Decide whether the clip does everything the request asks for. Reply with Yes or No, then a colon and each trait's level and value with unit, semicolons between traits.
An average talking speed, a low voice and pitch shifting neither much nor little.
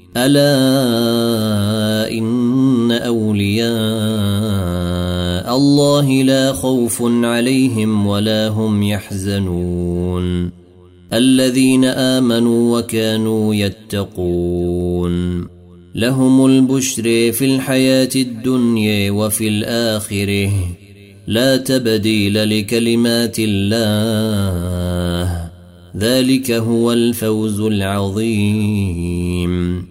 No: slow, 60 wpm; low, 110 Hz; average, 3.4 semitones